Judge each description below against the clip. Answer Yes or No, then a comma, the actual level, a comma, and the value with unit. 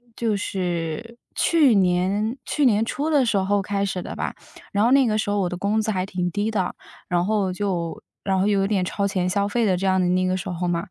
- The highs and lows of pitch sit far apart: No, average, 2.8 semitones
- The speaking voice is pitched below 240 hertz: Yes, high, 200 Hz